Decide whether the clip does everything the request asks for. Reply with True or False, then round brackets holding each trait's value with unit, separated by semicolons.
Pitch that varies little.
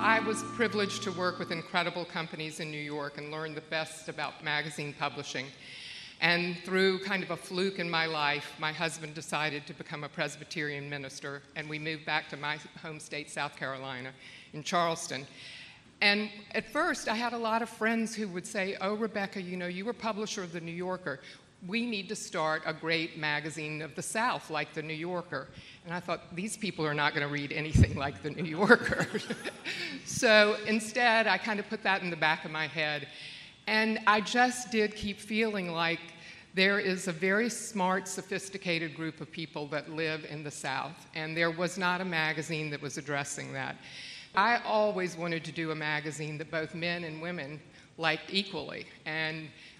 False (4.2 semitones)